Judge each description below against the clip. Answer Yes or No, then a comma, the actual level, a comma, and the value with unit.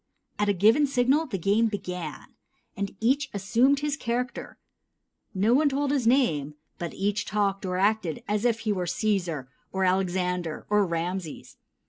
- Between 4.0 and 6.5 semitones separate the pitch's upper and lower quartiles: Yes, average, 5.0 semitones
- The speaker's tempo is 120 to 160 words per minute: Yes, average, 155 wpm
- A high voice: Yes, high, 205 Hz